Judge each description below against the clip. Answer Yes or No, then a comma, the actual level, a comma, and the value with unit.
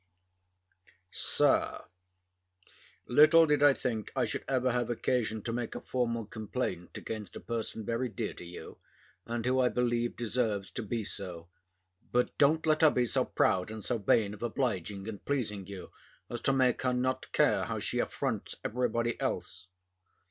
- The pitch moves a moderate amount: Yes, average, 3.2 semitones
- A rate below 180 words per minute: Yes, average, 170 wpm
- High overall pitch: No, low, 120 Hz